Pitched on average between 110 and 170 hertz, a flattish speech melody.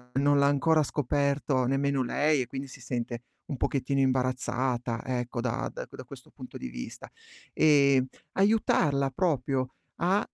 Yes: low, 135 Hz; narrow, 2.2 semitones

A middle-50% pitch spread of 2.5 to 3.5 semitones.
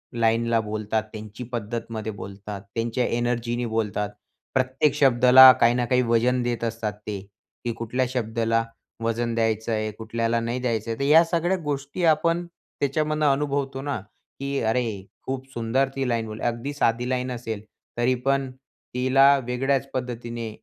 Yes: average, 2.8 semitones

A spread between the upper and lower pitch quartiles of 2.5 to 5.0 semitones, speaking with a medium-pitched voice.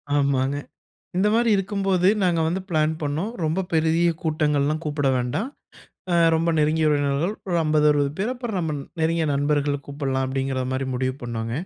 Yes: average, 3.5 semitones; medium, 155 Hz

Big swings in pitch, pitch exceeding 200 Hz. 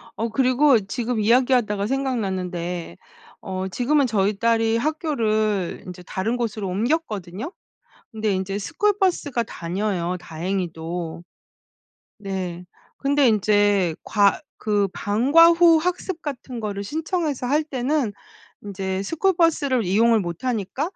Yes: wide, 6.2 semitones; high, 220 Hz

